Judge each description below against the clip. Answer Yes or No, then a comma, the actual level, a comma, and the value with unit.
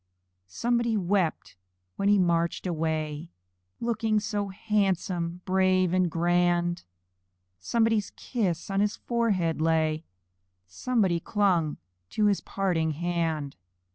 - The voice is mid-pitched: Yes, medium, 180 Hz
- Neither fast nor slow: No, slow, 105 wpm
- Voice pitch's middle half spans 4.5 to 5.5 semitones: No, average, 3.8 semitones